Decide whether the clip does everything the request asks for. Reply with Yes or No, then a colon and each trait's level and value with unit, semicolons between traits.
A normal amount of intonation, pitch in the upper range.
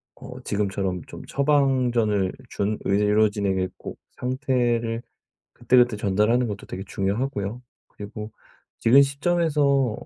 No: average, 4.3 semitones; low, 115 Hz